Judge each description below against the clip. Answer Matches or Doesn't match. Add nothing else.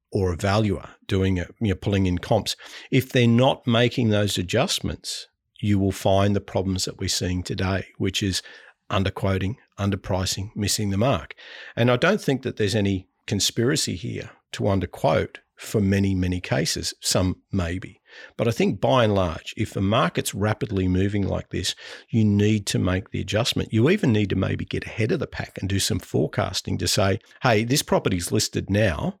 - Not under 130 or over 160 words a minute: Doesn't match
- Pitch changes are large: Doesn't match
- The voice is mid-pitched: Doesn't match